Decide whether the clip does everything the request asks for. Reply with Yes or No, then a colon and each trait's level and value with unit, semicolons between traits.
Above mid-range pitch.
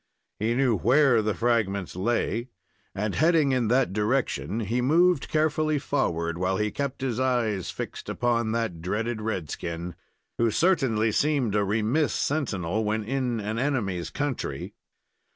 No: low, 115 Hz